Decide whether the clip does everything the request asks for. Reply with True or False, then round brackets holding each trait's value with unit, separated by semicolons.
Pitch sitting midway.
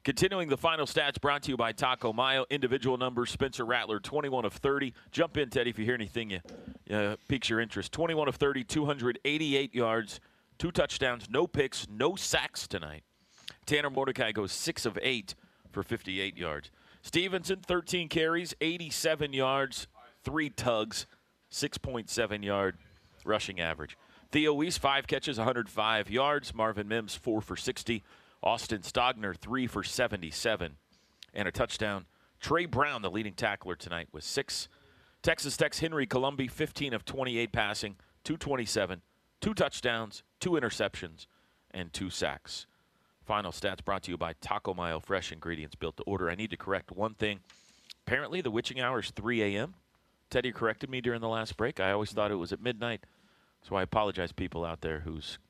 False (115 Hz)